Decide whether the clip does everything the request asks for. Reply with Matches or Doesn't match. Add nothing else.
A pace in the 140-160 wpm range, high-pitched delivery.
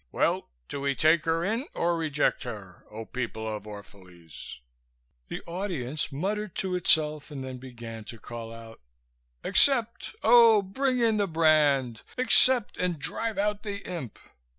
Doesn't match